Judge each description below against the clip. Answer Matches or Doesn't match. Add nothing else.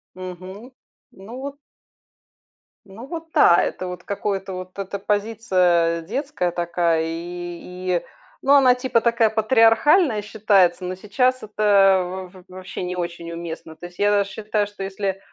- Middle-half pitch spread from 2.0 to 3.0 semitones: Doesn't match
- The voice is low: Doesn't match